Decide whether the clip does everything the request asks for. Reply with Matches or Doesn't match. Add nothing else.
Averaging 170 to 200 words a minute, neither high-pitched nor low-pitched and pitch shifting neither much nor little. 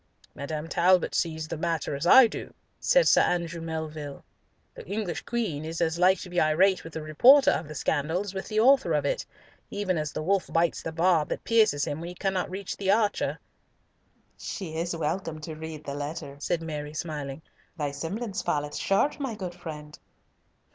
Matches